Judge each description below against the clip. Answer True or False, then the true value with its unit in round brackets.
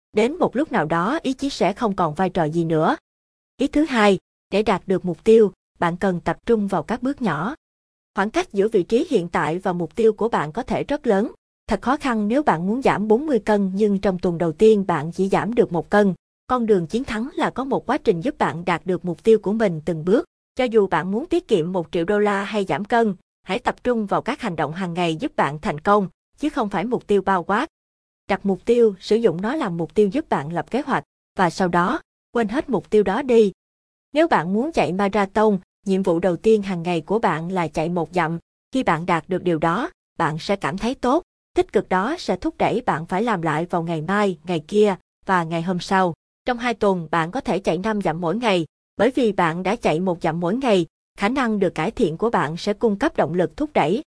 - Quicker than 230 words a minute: True (245 wpm)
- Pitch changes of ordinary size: True (4.4 semitones)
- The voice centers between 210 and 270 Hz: False (200 Hz)